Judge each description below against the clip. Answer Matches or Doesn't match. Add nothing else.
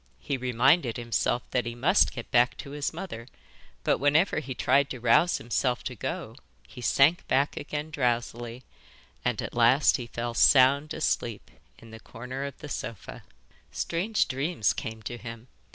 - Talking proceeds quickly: Doesn't match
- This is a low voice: Matches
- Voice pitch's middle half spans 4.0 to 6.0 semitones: Doesn't match